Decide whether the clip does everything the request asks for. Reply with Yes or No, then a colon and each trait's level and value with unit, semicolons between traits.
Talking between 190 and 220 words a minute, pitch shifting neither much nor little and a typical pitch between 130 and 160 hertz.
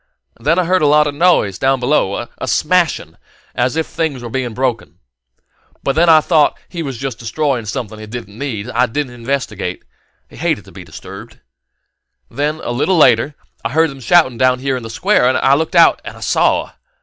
Yes: average, 200 wpm; average, 4.6 semitones; low, 135 Hz